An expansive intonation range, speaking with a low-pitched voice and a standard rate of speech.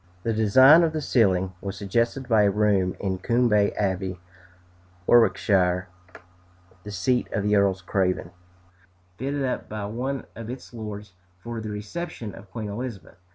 No: average, 3.8 semitones; low, 105 Hz; average, 150 wpm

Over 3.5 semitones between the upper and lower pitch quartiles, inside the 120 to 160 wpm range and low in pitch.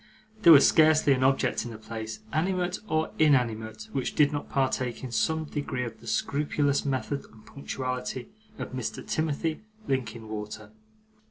Yes: average, 4.6 semitones; average, 150 wpm; low, 130 Hz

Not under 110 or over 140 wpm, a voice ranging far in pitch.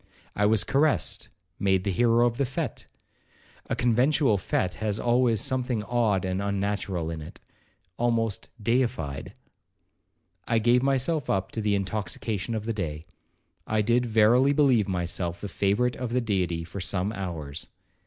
No: slow, 135 wpm; average, 4.2 semitones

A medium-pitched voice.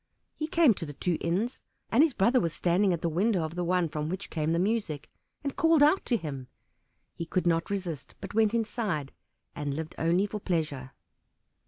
Yes: medium, 180 Hz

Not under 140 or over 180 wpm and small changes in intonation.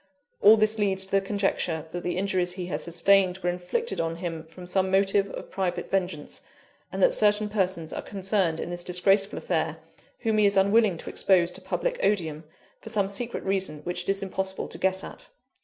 No: average, 200 wpm; narrow, 2.2 semitones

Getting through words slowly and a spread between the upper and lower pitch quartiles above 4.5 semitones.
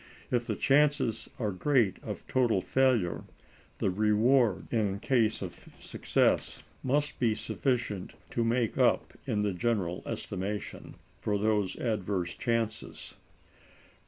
No: slow, 120 wpm; average, 3.5 semitones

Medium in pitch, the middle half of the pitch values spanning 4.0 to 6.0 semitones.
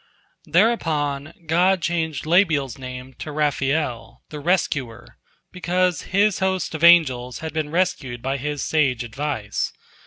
Yes: medium, 150 Hz; average, 4.5 semitones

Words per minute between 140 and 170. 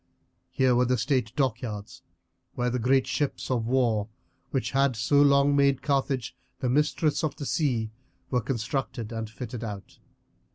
Yes: average, 155 wpm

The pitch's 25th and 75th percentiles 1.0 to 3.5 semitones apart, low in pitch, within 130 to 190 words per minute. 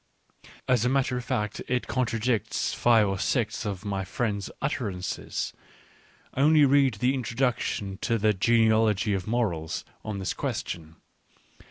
No: average, 4.0 semitones; low, 110 Hz; average, 140 wpm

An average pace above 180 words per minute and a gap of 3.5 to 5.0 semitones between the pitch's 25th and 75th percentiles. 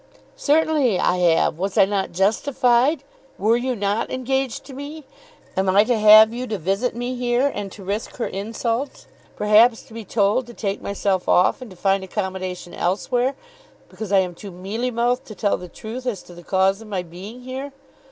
Yes: average, 190 wpm; average, 4.4 semitones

